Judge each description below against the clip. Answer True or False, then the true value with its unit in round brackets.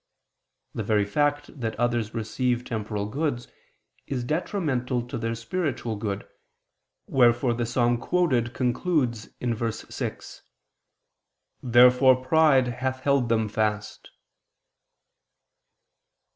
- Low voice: True (120 Hz)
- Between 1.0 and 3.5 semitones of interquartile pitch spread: True (2.4 semitones)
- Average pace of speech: False (100 wpm)